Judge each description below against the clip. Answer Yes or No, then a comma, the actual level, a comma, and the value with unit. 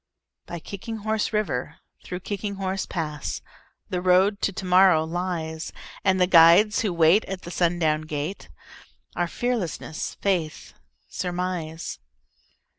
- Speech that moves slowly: Yes, slow, 120 wpm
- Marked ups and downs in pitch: No, average, 3.2 semitones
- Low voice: No, medium, 180 Hz